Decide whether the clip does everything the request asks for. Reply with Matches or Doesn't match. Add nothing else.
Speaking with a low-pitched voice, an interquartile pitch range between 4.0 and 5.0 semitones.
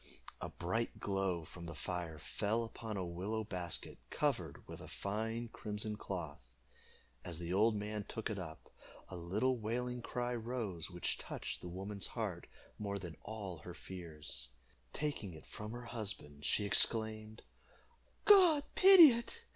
Matches